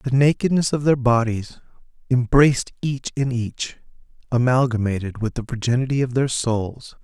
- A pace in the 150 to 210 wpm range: No, slow, 135 wpm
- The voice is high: No, low, 125 Hz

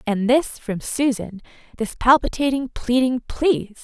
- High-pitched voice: Yes, high, 245 Hz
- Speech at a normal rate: No, slow, 110 wpm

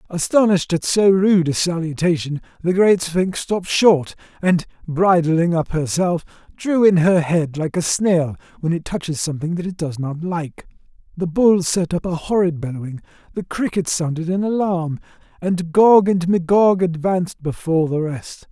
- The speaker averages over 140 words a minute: Yes, average, 165 wpm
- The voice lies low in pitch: No, medium, 170 Hz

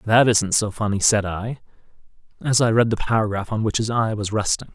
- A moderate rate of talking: No, fast, 215 wpm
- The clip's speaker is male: Yes, male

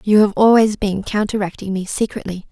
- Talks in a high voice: Yes, high, 205 Hz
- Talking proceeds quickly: No, average, 165 wpm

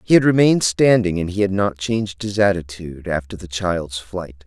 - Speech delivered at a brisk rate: No, average, 190 wpm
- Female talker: No, male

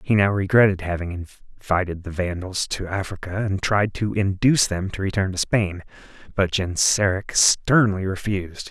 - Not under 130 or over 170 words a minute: Yes, average, 150 wpm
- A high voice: No, very low, 95 Hz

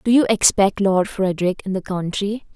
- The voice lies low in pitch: No, high, 195 Hz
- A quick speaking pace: No, average, 190 wpm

